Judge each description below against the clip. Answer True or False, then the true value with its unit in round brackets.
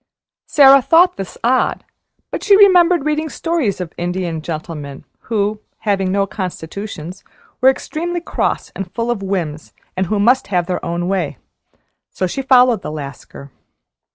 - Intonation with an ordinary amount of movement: False (7.3 semitones)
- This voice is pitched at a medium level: False (200 Hz)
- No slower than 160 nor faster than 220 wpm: False (150 wpm)